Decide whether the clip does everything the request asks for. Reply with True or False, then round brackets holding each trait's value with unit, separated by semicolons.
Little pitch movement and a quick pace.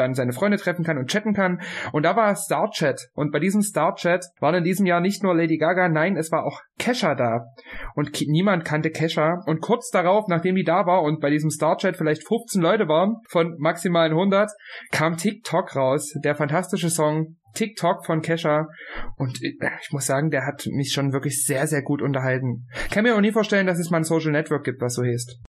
False (4.2 semitones; 215 wpm)